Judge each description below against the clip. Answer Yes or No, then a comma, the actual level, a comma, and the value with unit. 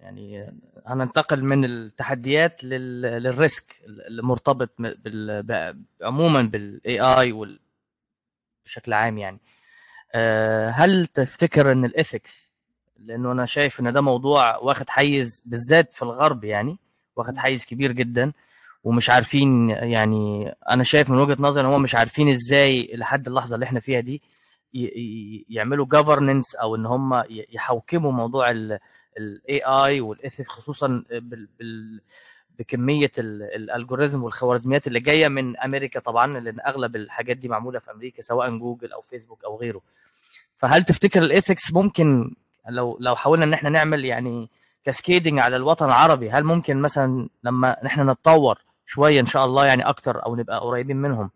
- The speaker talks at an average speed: No, fast, 145 wpm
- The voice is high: No, low, 125 Hz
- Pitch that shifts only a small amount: No, average, 3.3 semitones